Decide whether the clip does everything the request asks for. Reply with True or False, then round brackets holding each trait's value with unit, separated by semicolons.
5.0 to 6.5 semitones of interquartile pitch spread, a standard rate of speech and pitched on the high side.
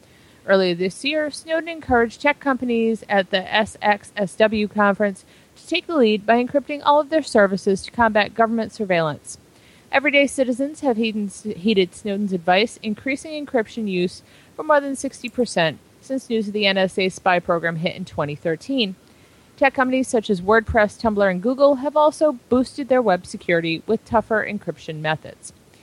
True (5.5 semitones; 155 wpm; 220 Hz)